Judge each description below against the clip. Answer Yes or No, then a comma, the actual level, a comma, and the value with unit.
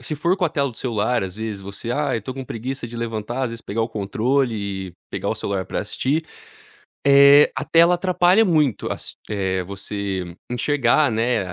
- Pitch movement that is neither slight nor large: No, wide, 5.8 semitones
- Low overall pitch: Yes, low, 115 Hz